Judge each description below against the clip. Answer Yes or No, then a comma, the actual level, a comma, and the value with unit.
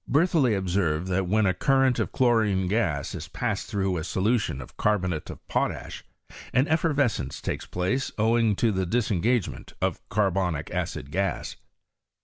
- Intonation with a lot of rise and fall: No, average, 4.8 semitones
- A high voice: No, low, 100 Hz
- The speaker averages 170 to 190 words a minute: No, average, 150 wpm